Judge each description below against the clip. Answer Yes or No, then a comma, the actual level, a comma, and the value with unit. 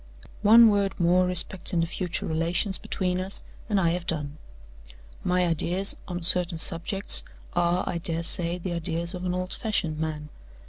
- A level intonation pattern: Yes, narrow, 1.8 semitones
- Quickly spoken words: No, average, 165 wpm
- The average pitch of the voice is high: No, medium, 175 Hz